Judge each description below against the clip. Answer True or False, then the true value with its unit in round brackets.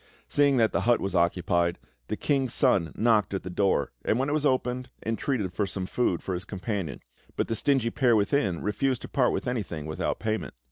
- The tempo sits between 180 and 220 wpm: True (205 wpm)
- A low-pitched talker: True (110 Hz)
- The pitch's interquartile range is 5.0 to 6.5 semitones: True (5.5 semitones)